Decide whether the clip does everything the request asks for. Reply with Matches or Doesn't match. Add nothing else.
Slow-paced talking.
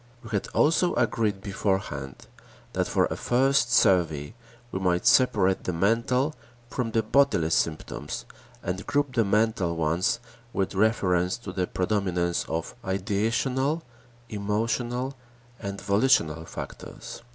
Matches